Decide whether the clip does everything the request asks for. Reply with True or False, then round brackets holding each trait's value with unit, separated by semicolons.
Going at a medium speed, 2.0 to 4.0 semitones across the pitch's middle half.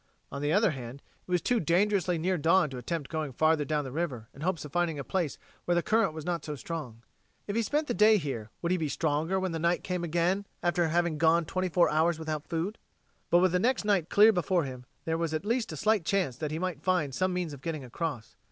False (245 wpm; 3.5 semitones)